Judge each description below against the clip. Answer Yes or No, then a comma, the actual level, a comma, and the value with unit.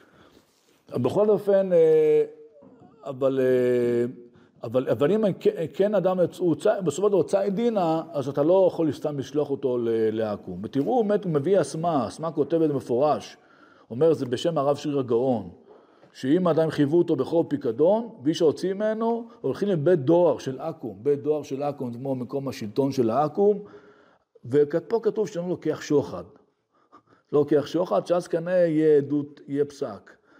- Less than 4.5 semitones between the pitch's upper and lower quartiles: No, average, 5.1 semitones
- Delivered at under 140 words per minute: No, average, 145 wpm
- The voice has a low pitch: No, medium, 155 Hz